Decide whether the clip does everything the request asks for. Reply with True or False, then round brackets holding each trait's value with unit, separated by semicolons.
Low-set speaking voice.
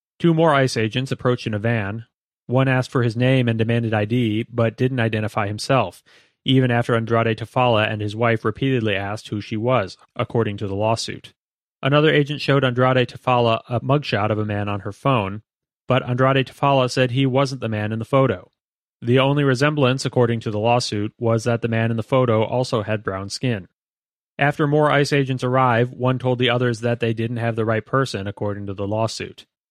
True (120 Hz)